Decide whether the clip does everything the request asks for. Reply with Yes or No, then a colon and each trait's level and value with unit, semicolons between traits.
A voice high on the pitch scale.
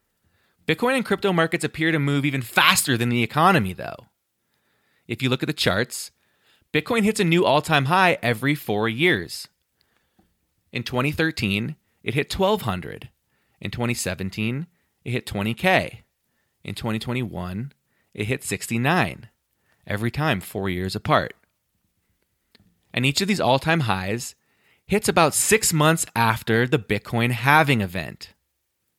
No: low, 130 Hz